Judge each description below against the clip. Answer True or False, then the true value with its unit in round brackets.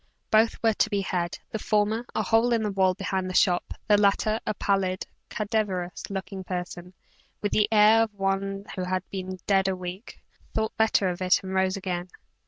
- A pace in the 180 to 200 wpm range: True (190 wpm)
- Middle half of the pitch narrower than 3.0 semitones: True (2.4 semitones)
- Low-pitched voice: False (195 Hz)